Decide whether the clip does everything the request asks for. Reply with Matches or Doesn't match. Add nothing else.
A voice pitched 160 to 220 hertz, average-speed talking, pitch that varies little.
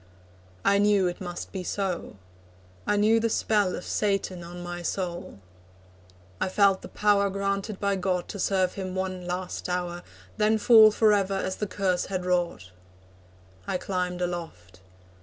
Matches